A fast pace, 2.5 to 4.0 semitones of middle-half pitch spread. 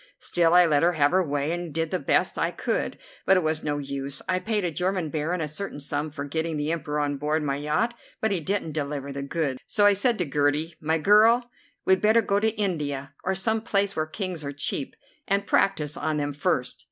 No: fast, 225 wpm; average, 4.7 semitones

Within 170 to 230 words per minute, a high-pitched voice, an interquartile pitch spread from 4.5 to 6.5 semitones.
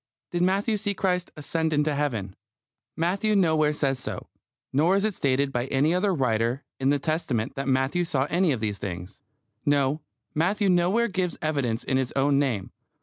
No: average, 175 wpm; medium, 150 Hz; average, 5.2 semitones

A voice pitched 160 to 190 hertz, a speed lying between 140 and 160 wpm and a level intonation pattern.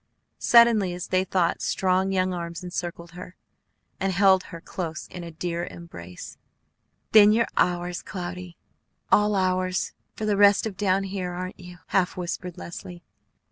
Yes: medium, 185 Hz; average, 150 wpm; narrow, 1.6 semitones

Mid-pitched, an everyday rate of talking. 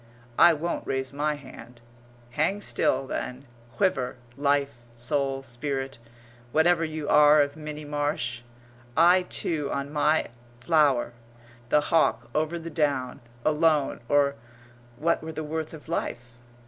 No: medium, 145 Hz; slow, 130 wpm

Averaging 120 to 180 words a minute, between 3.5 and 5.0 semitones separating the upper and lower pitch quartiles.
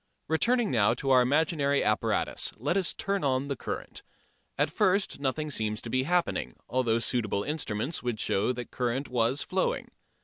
Yes: average, 165 wpm; average, 4.7 semitones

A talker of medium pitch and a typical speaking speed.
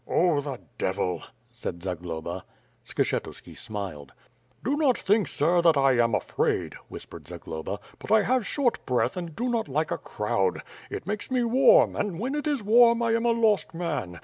Yes: medium, 175 Hz; average, 175 wpm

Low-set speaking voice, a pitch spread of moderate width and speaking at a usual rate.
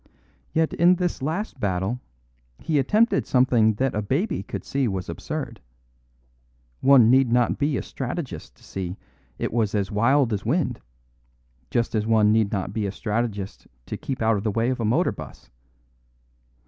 Yes: low, 115 Hz; average, 4.6 semitones; average, 170 wpm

